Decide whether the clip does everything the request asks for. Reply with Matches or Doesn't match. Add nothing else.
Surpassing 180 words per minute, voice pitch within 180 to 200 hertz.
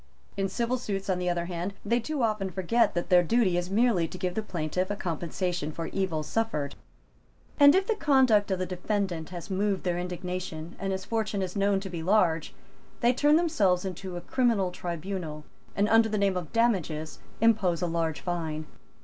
Matches